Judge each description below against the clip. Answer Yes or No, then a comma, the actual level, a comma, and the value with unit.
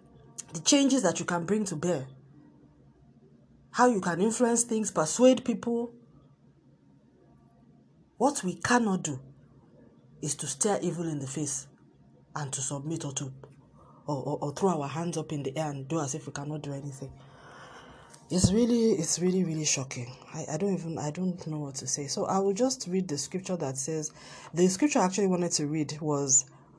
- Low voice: No, medium, 160 Hz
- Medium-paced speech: Yes, average, 180 wpm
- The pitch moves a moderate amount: Yes, average, 4.9 semitones